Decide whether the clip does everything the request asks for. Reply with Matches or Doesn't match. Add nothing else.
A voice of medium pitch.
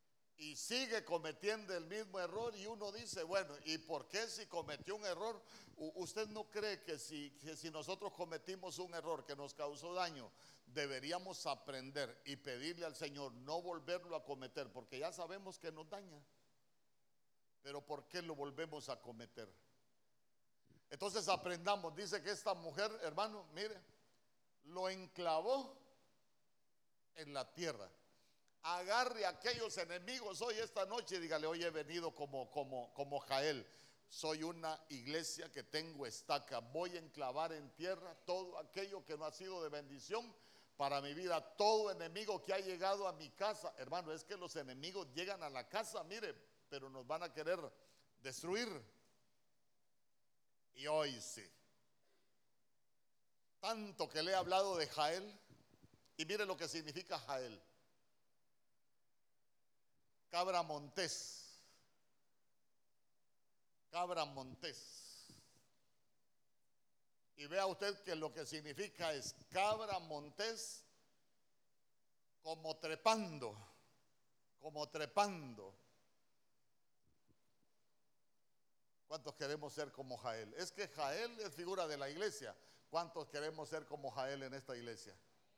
Matches